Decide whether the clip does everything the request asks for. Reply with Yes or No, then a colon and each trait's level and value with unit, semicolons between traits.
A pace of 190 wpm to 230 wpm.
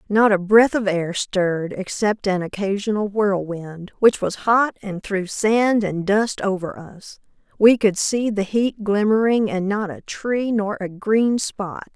No: average, 170 wpm